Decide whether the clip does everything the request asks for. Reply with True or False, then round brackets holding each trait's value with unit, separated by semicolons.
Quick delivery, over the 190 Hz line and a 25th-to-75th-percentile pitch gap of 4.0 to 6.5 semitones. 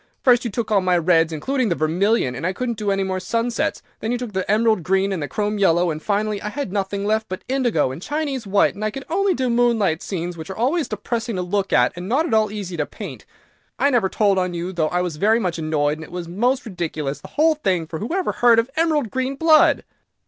True (250 wpm; 205 Hz; 5.3 semitones)